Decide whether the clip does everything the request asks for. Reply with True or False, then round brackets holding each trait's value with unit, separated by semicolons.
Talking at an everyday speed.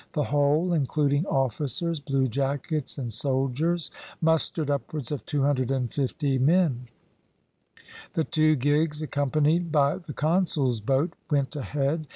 False (110 wpm)